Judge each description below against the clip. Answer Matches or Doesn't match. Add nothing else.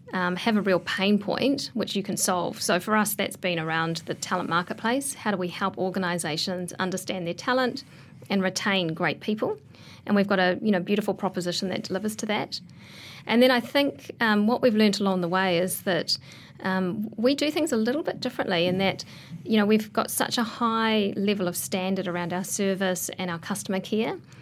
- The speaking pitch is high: Matches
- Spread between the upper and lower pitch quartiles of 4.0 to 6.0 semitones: Doesn't match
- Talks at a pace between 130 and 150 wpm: Doesn't match